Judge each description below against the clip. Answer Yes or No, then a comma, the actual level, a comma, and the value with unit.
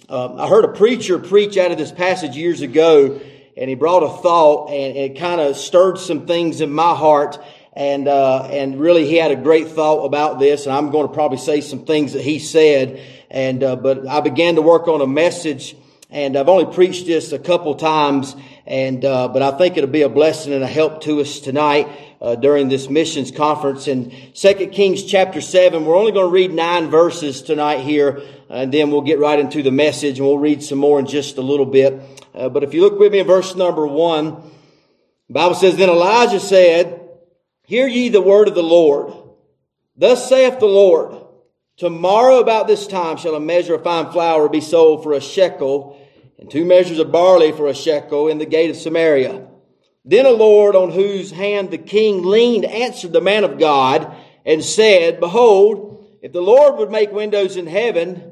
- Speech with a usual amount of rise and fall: Yes, average, 4.3 semitones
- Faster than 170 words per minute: Yes, fast, 205 wpm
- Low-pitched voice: No, medium, 155 Hz